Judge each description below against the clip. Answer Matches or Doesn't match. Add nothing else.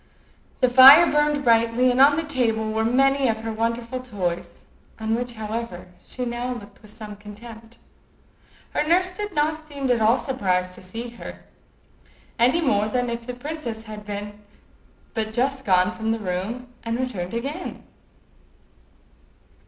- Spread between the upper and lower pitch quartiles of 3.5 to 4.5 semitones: Doesn't match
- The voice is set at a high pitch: Matches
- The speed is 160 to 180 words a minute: Doesn't match